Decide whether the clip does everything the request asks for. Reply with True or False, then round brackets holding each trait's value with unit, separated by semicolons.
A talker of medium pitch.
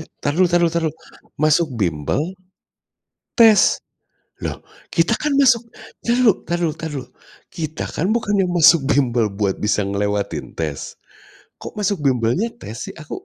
True (160 Hz)